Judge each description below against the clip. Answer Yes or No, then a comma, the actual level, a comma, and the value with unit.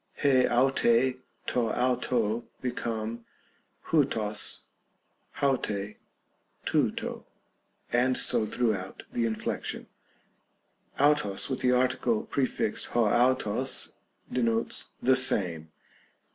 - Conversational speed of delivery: No, slow, 90 wpm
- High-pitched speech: No, low, 120 Hz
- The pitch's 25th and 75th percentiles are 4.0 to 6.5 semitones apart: No, average, 3.0 semitones